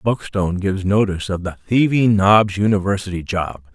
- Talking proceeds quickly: No, average, 145 wpm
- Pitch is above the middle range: No, low, 100 Hz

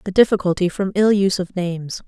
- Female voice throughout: Yes, female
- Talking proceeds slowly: No, fast, 205 wpm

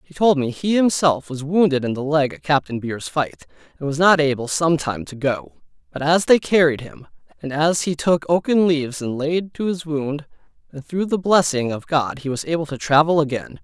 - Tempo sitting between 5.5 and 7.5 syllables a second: No, 5.1 syllables/s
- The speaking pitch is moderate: Yes, medium, 150 Hz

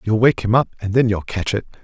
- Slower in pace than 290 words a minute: No, fast, 295 wpm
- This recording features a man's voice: Yes, male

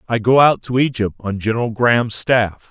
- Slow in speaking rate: No, average, 200 wpm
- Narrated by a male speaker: Yes, male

